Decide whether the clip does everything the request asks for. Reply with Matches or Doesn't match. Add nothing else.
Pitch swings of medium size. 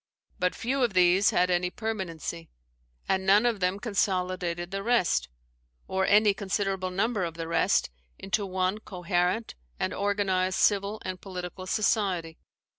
Doesn't match